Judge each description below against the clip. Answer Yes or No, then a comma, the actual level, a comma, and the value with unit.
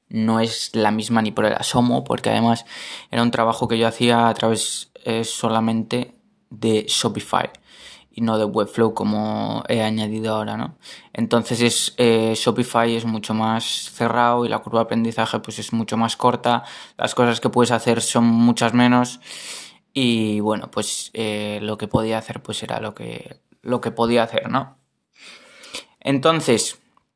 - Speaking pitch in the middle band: No, low, 115 Hz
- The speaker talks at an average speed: Yes, average, 165 wpm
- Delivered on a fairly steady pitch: Yes, narrow, 1.3 semitones